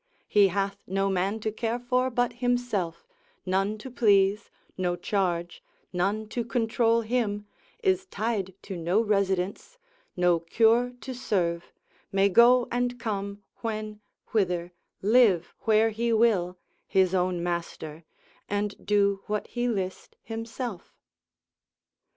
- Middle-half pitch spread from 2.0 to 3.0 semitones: No, average, 3.7 semitones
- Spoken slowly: Yes, slow, 125 wpm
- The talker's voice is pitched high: Yes, high, 205 Hz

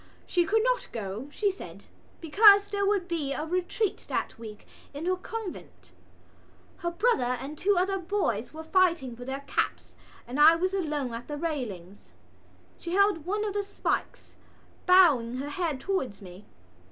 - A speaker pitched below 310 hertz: No, very high, 330 Hz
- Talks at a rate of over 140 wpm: Yes, average, 165 wpm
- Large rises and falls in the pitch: Yes, wide, 6.9 semitones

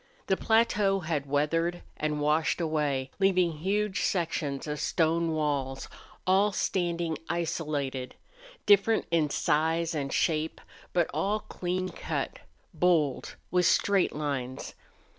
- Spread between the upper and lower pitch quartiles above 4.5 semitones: No, average, 3.5 semitones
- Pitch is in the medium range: Yes, medium, 165 Hz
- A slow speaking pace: Yes, slow, 115 wpm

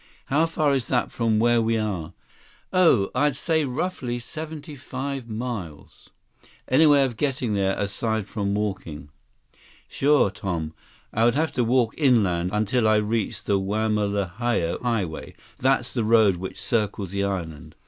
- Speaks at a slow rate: No, average, 150 wpm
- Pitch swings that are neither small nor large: Yes, average, 4.6 semitones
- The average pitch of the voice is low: Yes, low, 115 Hz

